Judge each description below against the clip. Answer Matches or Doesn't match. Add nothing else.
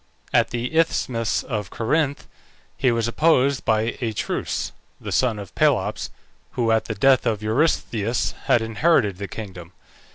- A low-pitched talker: Matches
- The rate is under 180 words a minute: Matches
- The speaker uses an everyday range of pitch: Matches